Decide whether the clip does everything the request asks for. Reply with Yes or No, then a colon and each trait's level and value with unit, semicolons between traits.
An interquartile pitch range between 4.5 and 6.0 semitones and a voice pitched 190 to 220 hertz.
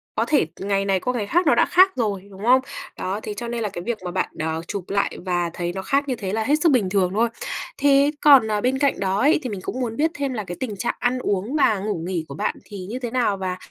Yes: average, 5.1 semitones; high, 215 Hz